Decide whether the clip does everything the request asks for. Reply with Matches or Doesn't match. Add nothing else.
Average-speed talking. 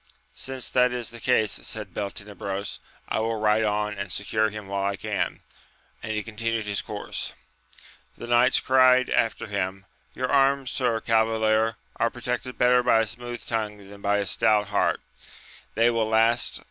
Matches